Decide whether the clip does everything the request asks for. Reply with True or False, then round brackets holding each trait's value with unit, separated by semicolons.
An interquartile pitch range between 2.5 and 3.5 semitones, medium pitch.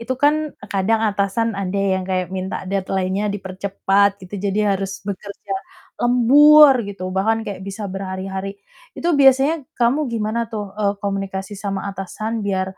False (2.8 semitones; 200 Hz)